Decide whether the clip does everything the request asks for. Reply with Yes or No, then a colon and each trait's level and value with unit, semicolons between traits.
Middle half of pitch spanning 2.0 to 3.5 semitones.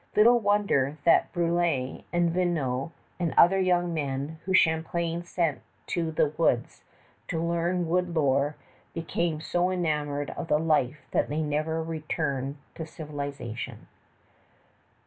Yes: average, 2.9 semitones